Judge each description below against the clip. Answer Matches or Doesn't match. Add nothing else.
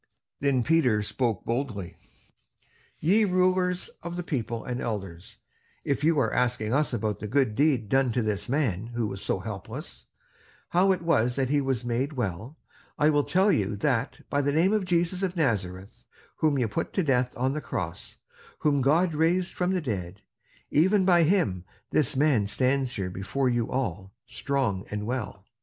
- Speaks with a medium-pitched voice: Doesn't match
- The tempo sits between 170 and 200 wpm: Matches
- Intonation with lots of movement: Matches